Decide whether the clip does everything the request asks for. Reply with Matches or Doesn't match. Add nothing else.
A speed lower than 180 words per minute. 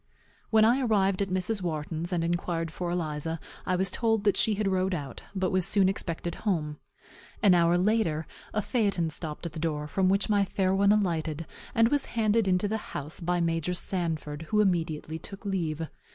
Doesn't match